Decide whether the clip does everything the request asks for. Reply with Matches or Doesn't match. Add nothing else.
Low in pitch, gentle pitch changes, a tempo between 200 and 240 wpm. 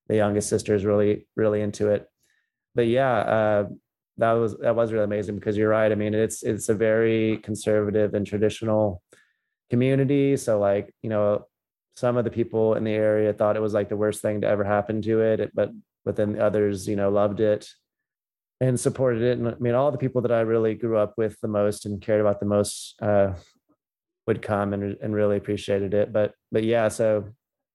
Matches